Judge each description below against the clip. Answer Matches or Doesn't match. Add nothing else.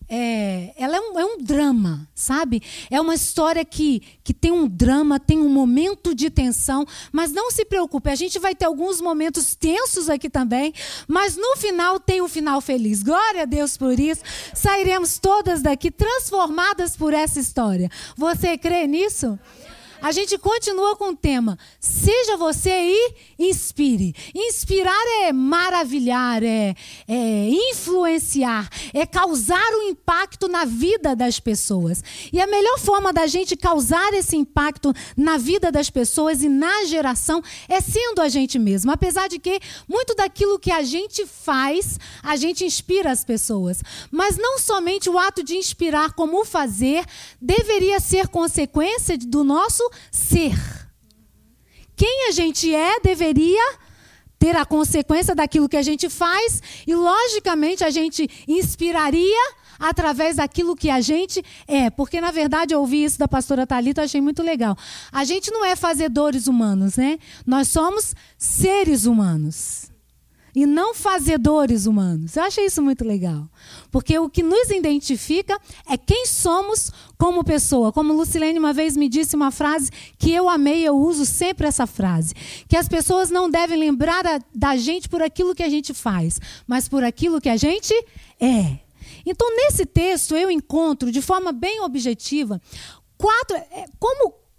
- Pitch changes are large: Doesn't match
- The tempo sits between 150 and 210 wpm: Matches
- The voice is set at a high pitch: Matches